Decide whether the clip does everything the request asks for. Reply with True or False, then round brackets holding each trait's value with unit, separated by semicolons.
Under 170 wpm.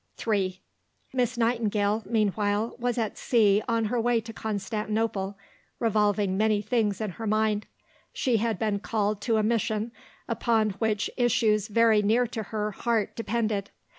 True (145 wpm)